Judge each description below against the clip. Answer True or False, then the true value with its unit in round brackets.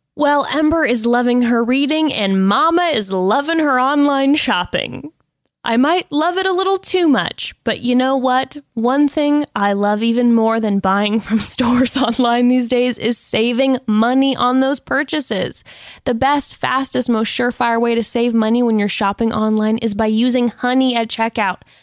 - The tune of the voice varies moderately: True (3.5 semitones)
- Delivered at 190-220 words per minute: False (175 wpm)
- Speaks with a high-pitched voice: True (245 Hz)